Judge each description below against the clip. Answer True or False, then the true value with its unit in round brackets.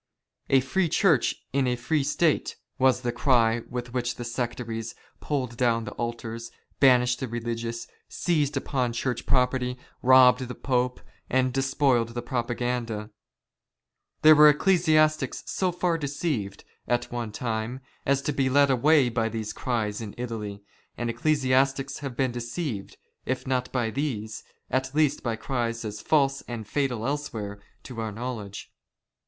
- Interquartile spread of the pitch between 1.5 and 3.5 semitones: True (2.8 semitones)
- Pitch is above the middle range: False (125 Hz)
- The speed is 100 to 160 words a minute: True (150 wpm)